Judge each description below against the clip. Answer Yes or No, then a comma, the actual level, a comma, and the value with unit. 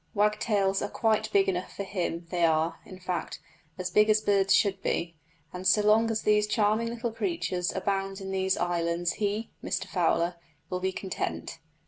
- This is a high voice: Yes, high, 195 Hz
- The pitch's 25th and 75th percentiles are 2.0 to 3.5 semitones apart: Yes, average, 2.8 semitones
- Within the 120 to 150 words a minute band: No, average, 175 wpm